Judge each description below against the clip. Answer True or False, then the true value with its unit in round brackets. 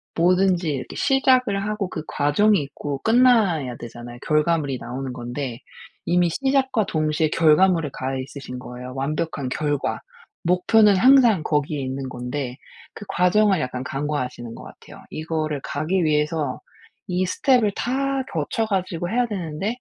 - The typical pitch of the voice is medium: True (160 Hz)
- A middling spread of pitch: False (6.6 semitones)